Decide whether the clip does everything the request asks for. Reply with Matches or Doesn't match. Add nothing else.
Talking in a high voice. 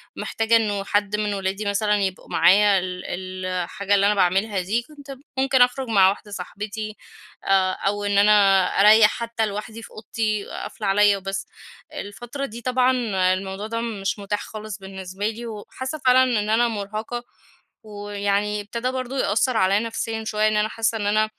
Matches